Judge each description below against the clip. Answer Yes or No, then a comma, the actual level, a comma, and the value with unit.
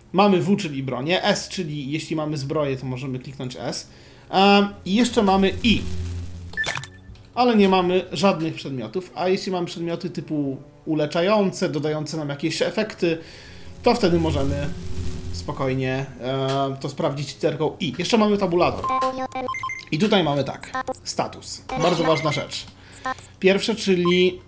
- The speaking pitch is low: No, medium, 165 Hz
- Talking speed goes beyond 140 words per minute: No, average, 130 wpm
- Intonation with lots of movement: Yes, wide, 6.1 semitones